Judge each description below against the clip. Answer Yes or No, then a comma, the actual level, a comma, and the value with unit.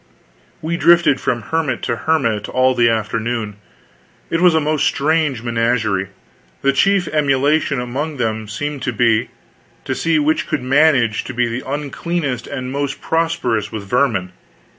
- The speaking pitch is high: No, low, 130 Hz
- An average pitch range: Yes, average, 4.9 semitones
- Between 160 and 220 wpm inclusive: No, average, 150 wpm